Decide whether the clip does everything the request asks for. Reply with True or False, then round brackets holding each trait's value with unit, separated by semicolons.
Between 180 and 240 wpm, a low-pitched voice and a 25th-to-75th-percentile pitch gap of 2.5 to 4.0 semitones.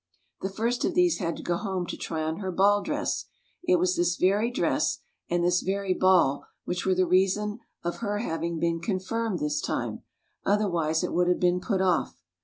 False (200 wpm; 185 Hz; 3.2 semitones)